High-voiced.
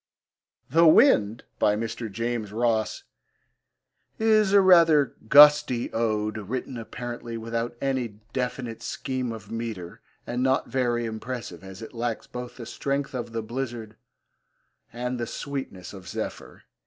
No: low, 120 Hz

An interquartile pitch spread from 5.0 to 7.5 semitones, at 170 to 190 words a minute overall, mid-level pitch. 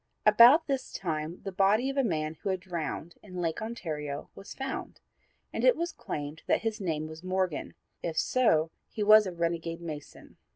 Yes: average, 5.3 semitones; average, 180 wpm; medium, 180 Hz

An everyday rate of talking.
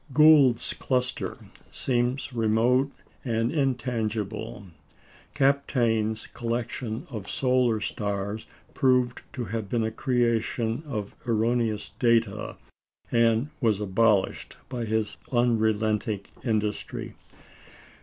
No: slow, 90 wpm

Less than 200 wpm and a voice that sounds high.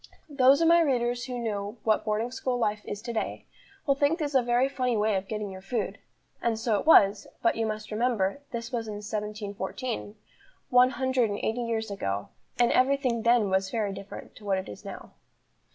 No: fast, 205 wpm; high, 230 Hz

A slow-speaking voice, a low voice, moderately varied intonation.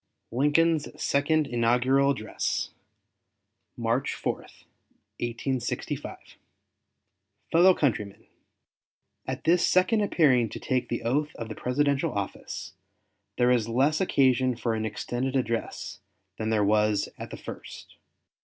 Yes: slow, 115 wpm; low, 125 Hz; average, 4.1 semitones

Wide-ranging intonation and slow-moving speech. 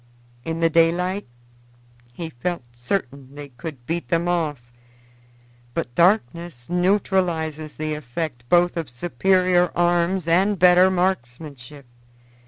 No: average, 3.9 semitones; slow, 110 wpm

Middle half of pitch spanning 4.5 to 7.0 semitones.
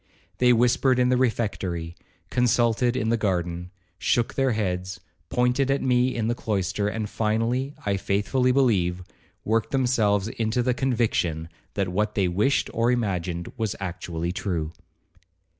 Yes: average, 5.1 semitones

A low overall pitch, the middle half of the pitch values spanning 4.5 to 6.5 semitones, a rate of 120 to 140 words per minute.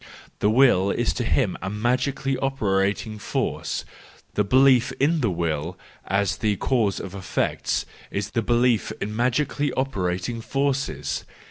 Yes: low, 115 Hz; average, 5.1 semitones; slow, 135 wpm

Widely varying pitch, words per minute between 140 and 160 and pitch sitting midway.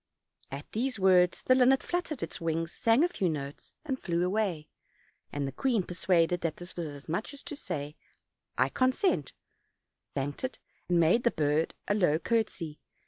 No: wide, 7.2 semitones; average, 175 wpm; medium, 180 Hz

